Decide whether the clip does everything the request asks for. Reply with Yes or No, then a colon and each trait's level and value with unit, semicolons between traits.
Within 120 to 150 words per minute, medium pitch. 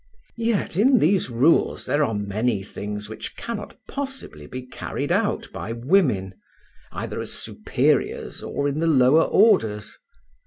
No: average, 140 wpm; low, 130 Hz